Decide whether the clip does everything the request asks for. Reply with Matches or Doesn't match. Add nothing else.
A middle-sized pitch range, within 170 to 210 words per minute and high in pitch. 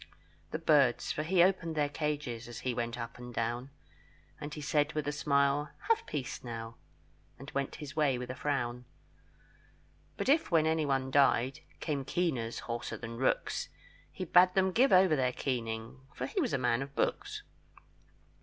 Doesn't match